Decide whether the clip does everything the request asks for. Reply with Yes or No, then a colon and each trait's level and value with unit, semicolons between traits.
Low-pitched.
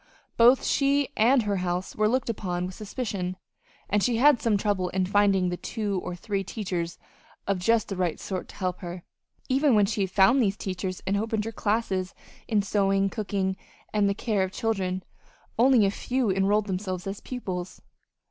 No: high, 200 Hz